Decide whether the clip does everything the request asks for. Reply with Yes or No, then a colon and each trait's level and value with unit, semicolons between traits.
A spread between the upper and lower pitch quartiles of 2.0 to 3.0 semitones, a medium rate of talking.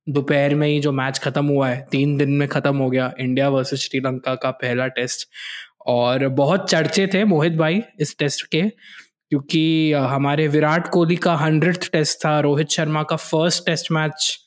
Yes: average, 2.7 semitones; average, 180 wpm